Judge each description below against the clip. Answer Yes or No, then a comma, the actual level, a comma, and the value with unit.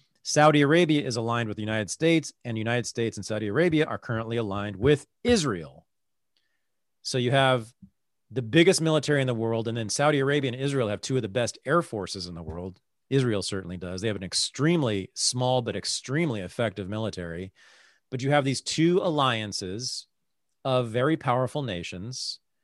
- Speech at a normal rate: Yes, average, 180 wpm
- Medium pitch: No, low, 120 Hz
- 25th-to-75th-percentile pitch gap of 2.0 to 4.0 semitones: No, average, 5.3 semitones